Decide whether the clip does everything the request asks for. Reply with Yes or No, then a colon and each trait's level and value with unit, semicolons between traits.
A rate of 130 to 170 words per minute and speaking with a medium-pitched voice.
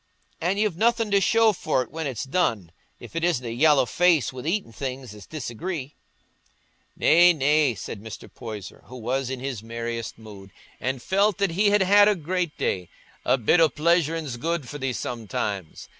No: average, 180 wpm; medium, 145 Hz